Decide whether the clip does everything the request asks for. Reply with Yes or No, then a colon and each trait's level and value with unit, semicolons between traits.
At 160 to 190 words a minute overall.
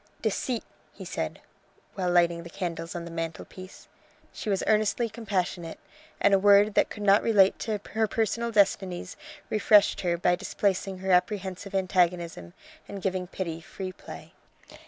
No: average, 150 wpm